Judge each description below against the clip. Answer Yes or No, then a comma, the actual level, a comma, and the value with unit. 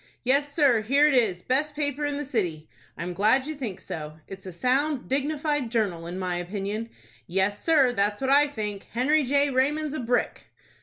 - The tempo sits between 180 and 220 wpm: Yes, average, 195 wpm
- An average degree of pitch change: No, wide, 6.4 semitones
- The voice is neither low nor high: No, very high, 250 Hz